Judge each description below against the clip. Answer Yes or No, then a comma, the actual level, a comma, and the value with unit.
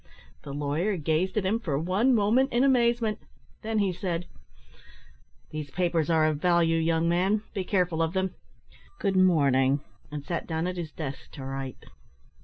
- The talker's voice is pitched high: No, medium, 175 Hz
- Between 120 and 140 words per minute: No, average, 170 wpm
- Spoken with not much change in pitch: No, average, 4.2 semitones